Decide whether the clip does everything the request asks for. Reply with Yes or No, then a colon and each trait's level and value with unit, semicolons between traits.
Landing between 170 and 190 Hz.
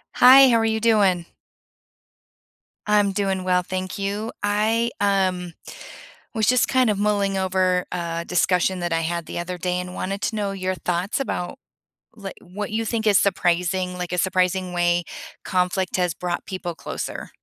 Yes: medium, 185 Hz